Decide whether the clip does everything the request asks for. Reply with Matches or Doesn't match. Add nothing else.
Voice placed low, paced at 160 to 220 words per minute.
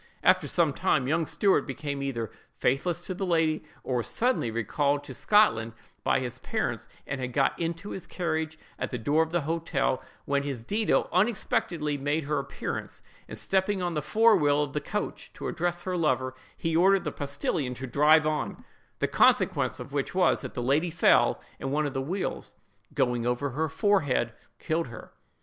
Doesn't match